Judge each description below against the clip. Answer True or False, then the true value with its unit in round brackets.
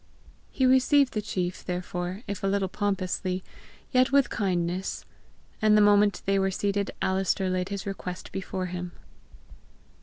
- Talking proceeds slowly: False (145 wpm)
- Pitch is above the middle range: True (195 Hz)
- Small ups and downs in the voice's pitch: True (2.1 semitones)